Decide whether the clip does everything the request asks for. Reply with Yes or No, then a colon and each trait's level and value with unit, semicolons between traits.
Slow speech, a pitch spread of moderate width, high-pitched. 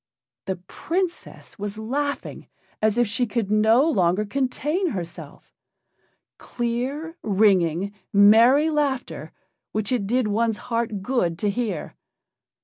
Yes: slow, 115 wpm; average, 4.5 semitones; high, 225 Hz